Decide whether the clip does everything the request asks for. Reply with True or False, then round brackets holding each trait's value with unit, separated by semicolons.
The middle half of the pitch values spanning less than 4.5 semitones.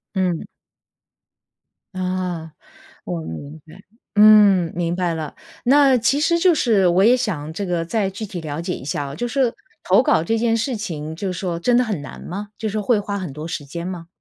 False (5.1 semitones)